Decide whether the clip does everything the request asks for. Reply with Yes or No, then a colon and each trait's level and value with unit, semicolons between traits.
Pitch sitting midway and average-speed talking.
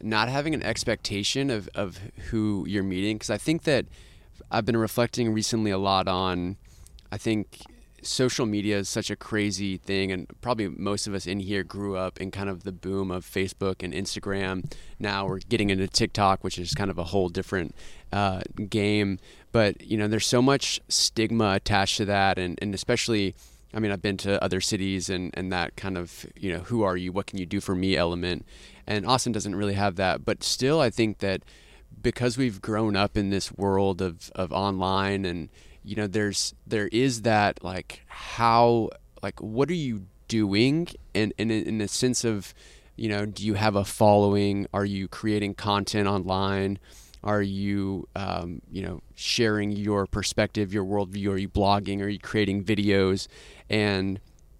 No: low, 100 Hz; average, 185 wpm